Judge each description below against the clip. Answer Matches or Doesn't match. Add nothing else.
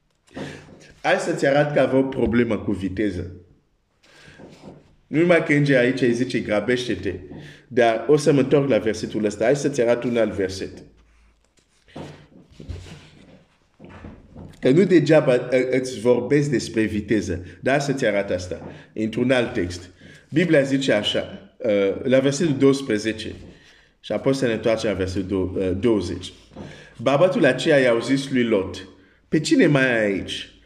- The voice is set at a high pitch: Doesn't match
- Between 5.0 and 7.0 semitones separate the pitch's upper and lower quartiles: Matches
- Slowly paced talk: Doesn't match